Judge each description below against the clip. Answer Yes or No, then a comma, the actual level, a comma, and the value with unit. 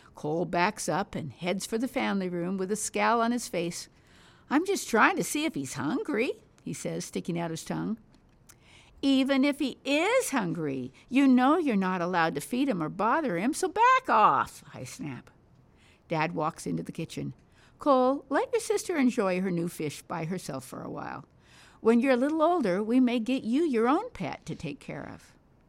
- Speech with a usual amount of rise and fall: No, wide, 7.6 semitones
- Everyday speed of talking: Yes, average, 195 wpm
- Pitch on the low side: No, high, 240 Hz